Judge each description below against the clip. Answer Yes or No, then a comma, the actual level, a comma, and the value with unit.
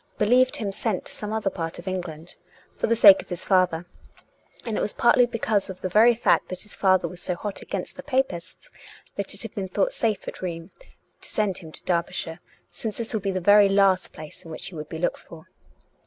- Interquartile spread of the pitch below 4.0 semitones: Yes, average, 3.5 semitones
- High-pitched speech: Yes, high, 195 Hz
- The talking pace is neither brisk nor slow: No, fast, 230 wpm